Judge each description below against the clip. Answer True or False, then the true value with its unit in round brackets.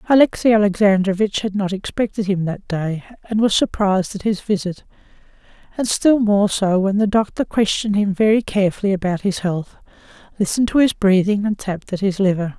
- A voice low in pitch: False (200 Hz)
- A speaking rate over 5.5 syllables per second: True (5.7 syllables/s)